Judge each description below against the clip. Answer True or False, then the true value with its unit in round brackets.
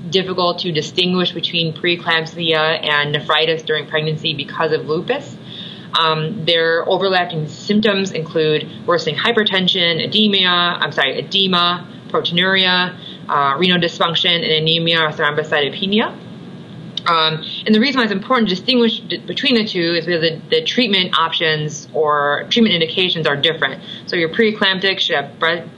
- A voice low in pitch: False (175 Hz)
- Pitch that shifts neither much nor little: True (3.3 semitones)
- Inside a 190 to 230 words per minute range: False (140 wpm)